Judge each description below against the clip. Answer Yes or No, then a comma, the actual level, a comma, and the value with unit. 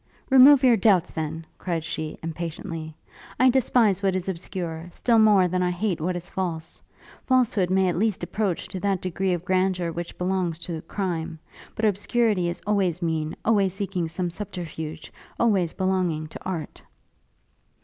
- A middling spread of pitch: Yes, average, 3.2 semitones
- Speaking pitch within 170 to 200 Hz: Yes, medium, 185 Hz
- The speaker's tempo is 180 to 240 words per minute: No, average, 160 wpm